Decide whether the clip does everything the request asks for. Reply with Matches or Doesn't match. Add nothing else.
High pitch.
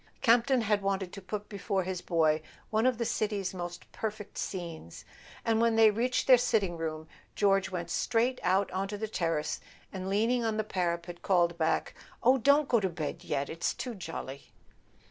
Matches